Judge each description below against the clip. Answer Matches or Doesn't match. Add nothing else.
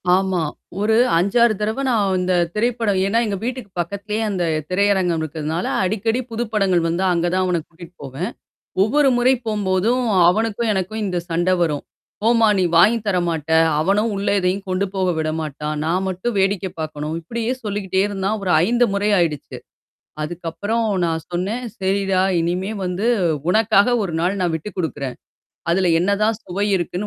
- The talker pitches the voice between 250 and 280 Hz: Doesn't match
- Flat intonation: Doesn't match